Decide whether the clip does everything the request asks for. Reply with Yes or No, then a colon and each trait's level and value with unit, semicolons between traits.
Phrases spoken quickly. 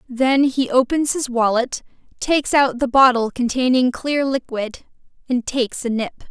No: average, 150 wpm